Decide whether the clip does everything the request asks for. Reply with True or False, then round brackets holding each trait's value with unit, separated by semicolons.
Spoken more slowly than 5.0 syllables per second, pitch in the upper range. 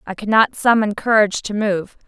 False (5.4 syllables/s; 210 Hz)